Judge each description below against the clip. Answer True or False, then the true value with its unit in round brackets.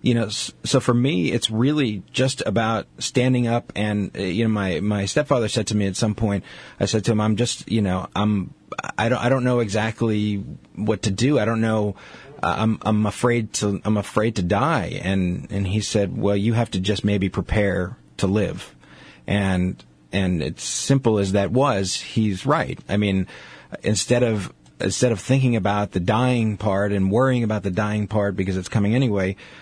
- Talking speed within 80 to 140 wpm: False (190 wpm)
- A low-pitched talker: True (105 Hz)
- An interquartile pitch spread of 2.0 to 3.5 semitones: True (2.9 semitones)